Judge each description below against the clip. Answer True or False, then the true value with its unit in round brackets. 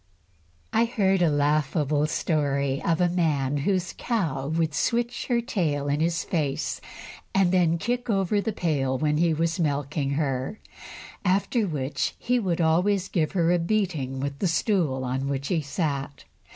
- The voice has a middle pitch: True (160 Hz)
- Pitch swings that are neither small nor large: True (4.9 semitones)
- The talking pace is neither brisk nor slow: True (160 wpm)